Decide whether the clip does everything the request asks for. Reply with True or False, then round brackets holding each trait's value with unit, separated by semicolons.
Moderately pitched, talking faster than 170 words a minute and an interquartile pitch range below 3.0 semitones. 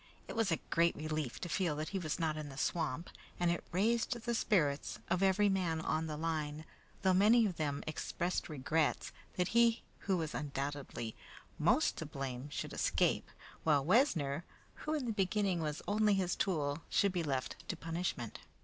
False (165 Hz; 180 wpm; 4.5 semitones)